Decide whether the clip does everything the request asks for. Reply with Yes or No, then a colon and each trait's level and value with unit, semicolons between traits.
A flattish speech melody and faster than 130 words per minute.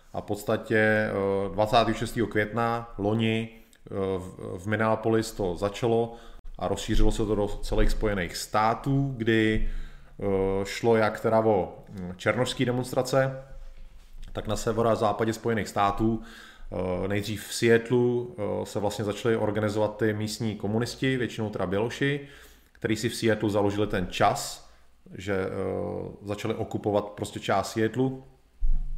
No: narrow, 2.2 semitones; average, 120 wpm